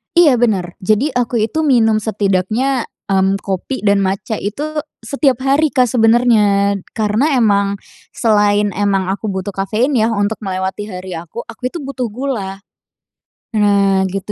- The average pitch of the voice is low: No, high, 210 Hz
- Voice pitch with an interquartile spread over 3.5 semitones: Yes, average, 3.9 semitones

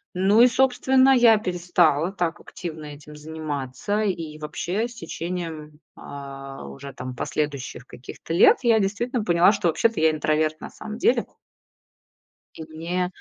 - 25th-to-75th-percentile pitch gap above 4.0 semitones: Yes, wide, 5.5 semitones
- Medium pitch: Yes, medium, 170 Hz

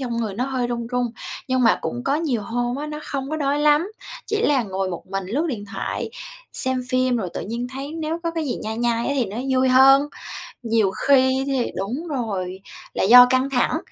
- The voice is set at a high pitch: Yes, very high, 255 Hz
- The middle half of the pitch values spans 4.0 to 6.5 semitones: No, average, 3.4 semitones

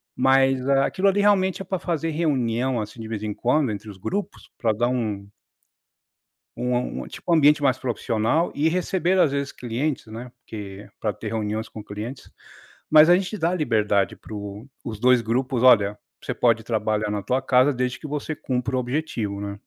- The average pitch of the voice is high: No, low, 125 Hz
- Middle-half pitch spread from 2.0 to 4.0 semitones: No, wide, 5.5 semitones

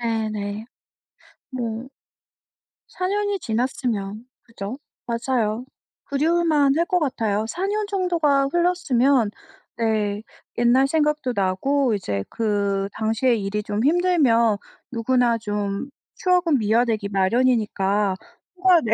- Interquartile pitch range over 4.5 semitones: Yes, wide, 5.6 semitones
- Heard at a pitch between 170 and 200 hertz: No, high, 235 Hz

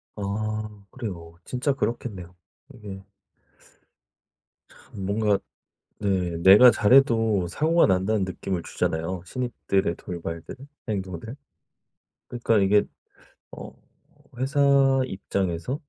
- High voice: No, low, 100 Hz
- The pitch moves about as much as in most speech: Yes, average, 3.8 semitones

